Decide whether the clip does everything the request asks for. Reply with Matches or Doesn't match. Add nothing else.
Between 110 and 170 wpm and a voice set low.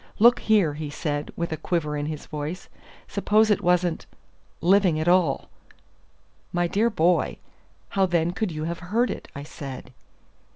Doesn't match